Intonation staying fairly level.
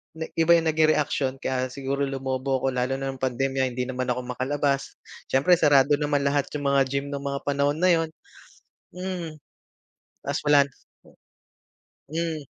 Yes: narrow, 2.3 semitones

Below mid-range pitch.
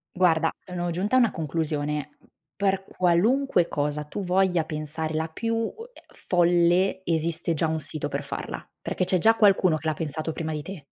No: medium, 170 Hz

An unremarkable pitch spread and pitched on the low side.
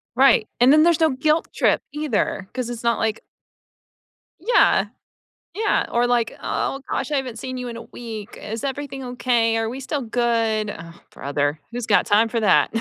No: average, 3.4 semitones; high, 240 Hz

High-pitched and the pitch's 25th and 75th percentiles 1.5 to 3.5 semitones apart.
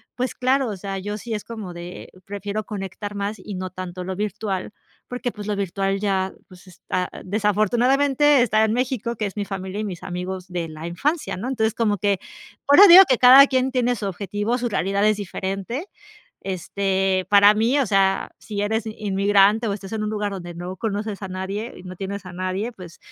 Yes: high, 205 Hz; average, 2.8 semitones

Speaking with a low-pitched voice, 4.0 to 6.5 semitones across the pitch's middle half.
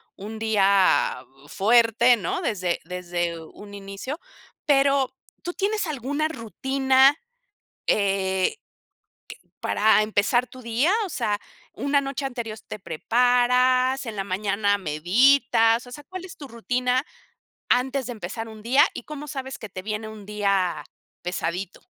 No: high, 230 Hz; average, 4.9 semitones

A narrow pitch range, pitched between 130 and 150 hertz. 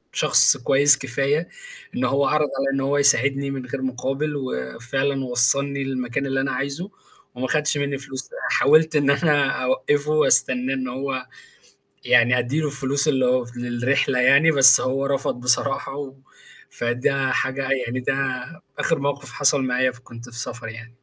Yes: narrow, 1.9 semitones; low, 135 Hz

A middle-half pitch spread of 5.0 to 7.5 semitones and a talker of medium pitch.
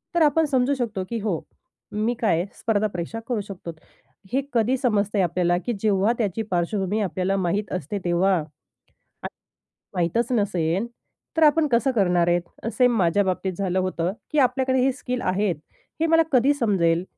No: average, 5.3 semitones; high, 205 Hz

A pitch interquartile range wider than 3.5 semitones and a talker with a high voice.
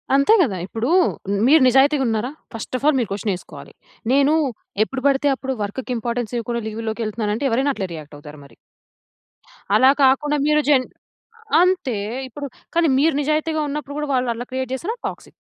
Yes: average, 4.3 semitones; very high, 260 Hz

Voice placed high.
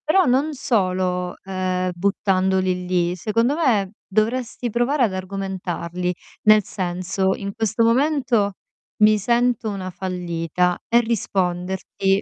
Yes: high, 195 Hz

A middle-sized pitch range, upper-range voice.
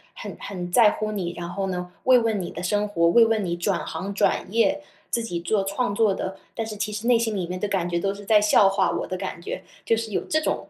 Yes: average, 3.5 semitones; high, 200 Hz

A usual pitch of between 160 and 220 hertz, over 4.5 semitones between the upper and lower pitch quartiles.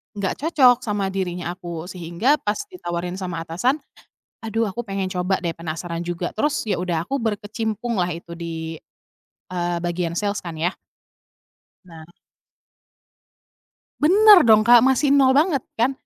Yes: high, 190 Hz; wide, 5.6 semitones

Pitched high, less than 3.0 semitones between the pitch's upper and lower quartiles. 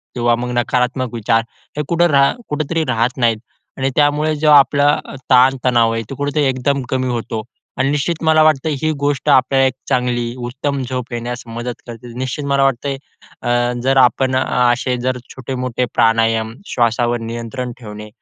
No: low, 125 Hz; narrow, 2.6 semitones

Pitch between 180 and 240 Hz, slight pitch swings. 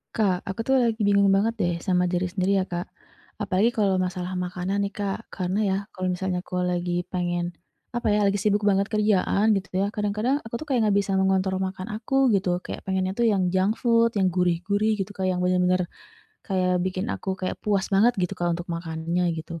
Yes: high, 190 Hz; narrow, 2.3 semitones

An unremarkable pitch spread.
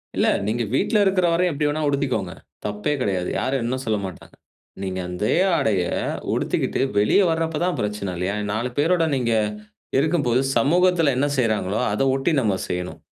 No: wide, 6.9 semitones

